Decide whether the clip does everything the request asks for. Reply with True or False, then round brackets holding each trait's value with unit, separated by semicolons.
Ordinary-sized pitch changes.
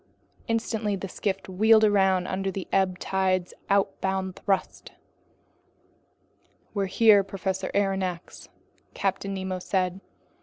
False (1.1 semitones)